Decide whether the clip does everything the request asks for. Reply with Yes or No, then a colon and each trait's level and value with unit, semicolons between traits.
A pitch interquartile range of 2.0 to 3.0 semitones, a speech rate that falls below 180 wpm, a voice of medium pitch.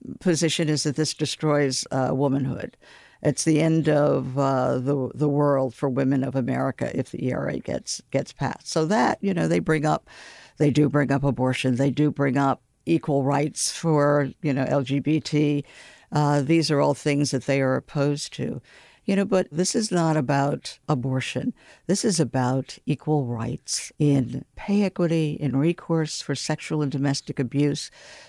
Yes: narrow, 2.5 semitones; average, 170 wpm; medium, 145 Hz